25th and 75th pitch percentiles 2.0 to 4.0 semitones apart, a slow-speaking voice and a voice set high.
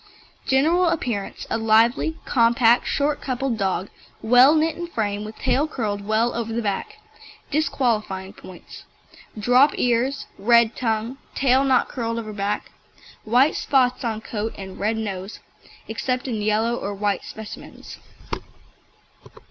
Yes: average, 3.6 semitones; slow, 130 wpm; high, 230 Hz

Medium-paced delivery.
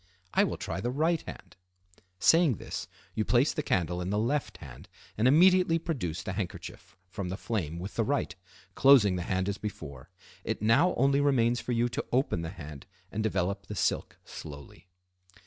Yes: average, 180 wpm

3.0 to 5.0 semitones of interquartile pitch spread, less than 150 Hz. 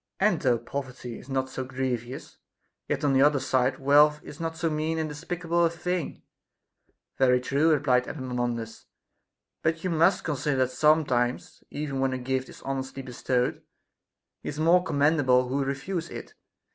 Yes: average, 3.7 semitones; medium, 140 Hz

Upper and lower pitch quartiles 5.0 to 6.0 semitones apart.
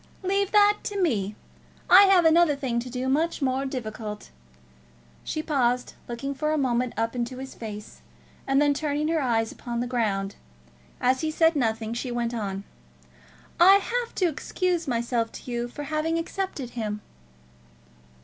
Yes: average, 5.3 semitones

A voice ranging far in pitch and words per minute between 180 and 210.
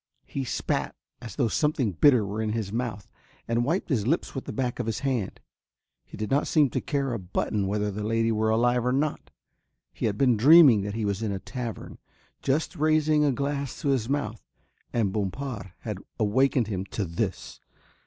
No: average, 4.7 semitones; average, 195 wpm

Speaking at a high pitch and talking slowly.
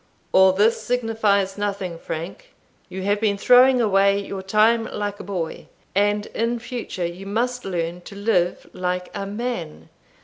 No: high, 200 Hz; average, 150 wpm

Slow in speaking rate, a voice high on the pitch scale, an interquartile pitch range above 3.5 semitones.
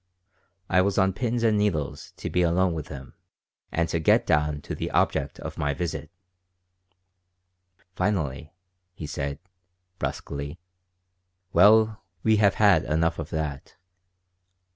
No: slow, 130 wpm; very low, 85 Hz; average, 5.1 semitones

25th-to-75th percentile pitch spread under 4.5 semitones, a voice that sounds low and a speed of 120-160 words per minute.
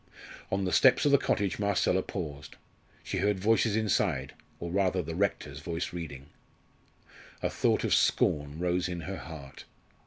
Yes: average, 3.8 semitones; very low, 90 Hz; average, 155 wpm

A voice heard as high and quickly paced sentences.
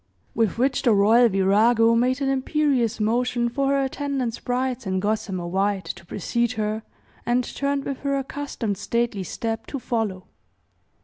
No: high, 235 Hz; average, 150 wpm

